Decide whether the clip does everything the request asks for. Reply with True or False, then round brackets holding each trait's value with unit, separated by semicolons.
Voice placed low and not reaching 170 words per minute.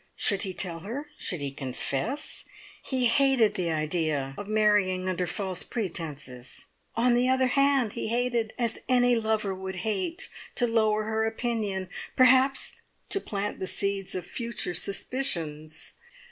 False (210 Hz; 145 wpm)